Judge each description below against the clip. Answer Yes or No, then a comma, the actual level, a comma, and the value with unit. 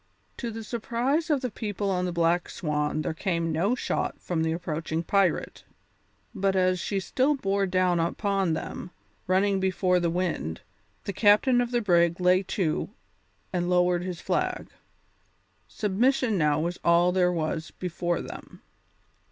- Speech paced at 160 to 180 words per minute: No, average, 150 wpm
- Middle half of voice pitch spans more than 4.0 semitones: No, average, 3.1 semitones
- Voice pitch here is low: No, medium, 180 Hz